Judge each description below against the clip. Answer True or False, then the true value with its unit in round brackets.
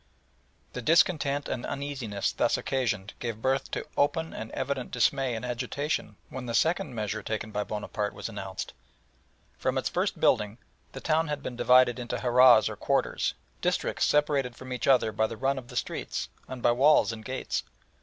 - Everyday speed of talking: True (175 wpm)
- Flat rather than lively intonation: False (3.5 semitones)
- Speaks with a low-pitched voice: True (125 Hz)